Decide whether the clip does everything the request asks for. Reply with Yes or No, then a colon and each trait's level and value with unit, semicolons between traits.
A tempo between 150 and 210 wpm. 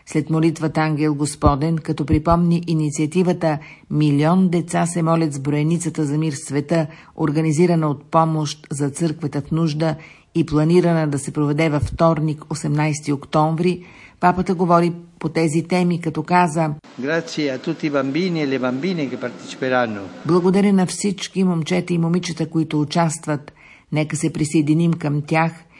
No: average, 120 wpm